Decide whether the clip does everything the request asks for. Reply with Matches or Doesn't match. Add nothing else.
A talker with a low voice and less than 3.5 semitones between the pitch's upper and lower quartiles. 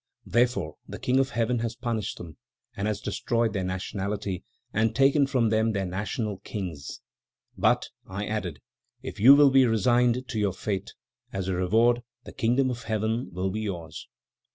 Doesn't match